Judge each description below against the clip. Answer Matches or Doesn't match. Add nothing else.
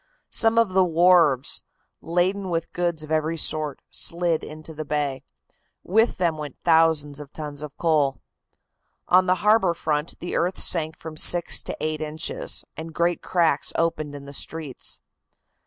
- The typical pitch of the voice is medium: Matches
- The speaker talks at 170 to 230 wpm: Doesn't match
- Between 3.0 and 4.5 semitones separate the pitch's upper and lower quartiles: Doesn't match